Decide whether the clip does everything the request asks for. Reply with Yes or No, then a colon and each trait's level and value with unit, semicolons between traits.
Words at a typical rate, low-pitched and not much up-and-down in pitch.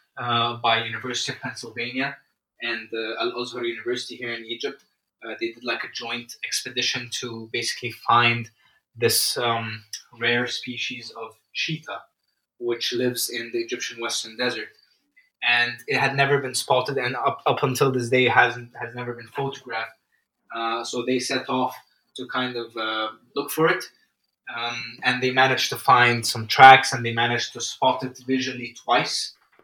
Yes: average, 160 wpm; low, 120 Hz; narrow, 1.7 semitones